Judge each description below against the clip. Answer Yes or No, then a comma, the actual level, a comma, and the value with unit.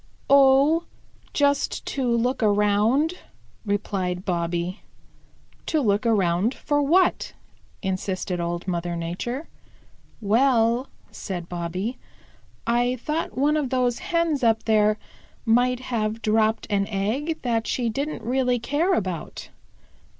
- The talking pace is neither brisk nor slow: No, slow, 115 wpm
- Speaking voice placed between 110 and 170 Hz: No, high, 230 Hz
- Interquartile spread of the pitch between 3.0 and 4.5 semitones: No, average, 5.3 semitones